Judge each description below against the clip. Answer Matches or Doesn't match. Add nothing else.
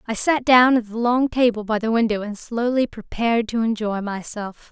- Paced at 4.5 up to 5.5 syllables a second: Matches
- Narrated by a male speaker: Doesn't match